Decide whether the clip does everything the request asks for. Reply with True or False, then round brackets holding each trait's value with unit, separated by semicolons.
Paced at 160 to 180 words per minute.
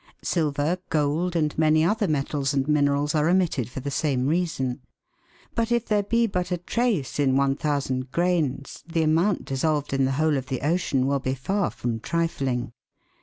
True (170 wpm)